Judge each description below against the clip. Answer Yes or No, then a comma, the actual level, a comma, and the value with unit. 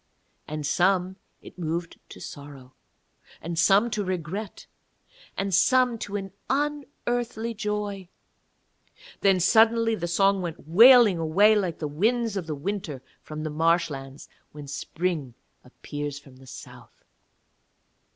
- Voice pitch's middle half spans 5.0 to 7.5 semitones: Yes, wide, 5.5 semitones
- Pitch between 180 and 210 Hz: Yes, medium, 185 Hz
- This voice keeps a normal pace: No, slow, 125 wpm